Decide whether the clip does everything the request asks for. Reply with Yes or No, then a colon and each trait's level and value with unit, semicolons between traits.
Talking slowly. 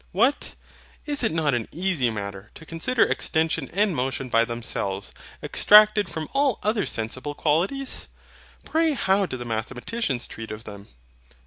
No: average, 145 wpm